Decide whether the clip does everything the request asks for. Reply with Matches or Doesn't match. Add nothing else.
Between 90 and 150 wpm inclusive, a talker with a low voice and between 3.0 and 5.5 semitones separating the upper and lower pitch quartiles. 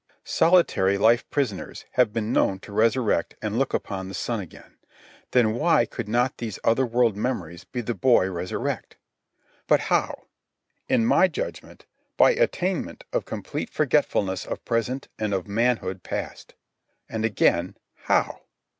Matches